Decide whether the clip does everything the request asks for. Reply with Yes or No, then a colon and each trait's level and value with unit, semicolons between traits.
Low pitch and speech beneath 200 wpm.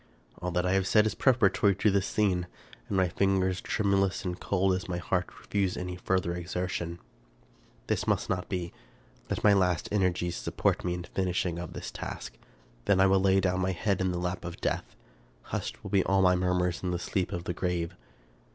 No: very low, 90 Hz; fast, 205 wpm